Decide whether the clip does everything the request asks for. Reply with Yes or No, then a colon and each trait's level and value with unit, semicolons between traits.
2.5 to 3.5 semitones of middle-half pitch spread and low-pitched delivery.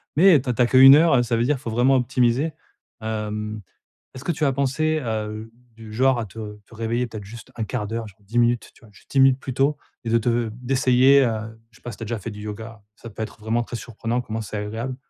Yes: average, 2.9 semitones; low, 115 Hz